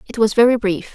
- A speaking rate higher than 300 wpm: No, fast, 255 wpm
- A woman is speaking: Yes, female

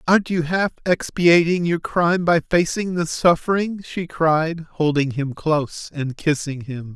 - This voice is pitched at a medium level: Yes, medium, 165 Hz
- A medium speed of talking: Yes, average, 155 wpm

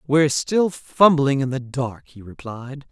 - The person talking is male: No, female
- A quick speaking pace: No, average, 165 wpm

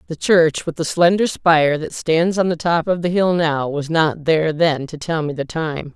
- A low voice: No, medium, 160 Hz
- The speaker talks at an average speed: No, fast, 240 wpm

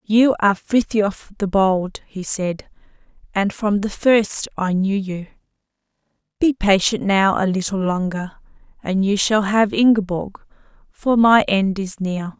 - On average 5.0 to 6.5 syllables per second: No, 4.0 syllables/s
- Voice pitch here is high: Yes, high, 200 Hz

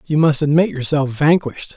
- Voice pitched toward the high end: No, medium, 150 Hz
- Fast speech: No, average, 170 wpm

